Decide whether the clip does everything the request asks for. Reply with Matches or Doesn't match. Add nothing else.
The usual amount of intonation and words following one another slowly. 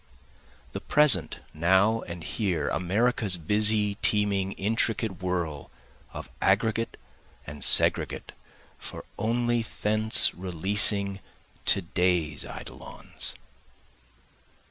Matches